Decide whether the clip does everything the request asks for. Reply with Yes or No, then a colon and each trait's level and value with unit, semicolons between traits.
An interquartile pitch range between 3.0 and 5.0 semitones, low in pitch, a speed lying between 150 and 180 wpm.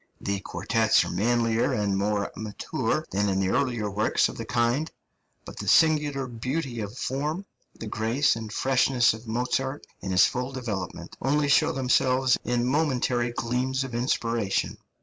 Yes: average, 3.3 semitones; low, 120 Hz; average, 155 wpm